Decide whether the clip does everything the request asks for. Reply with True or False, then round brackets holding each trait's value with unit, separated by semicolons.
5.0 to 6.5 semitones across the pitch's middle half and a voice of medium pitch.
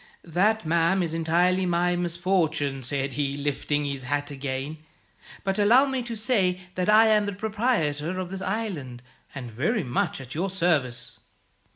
True (5.3 semitones; 175 Hz)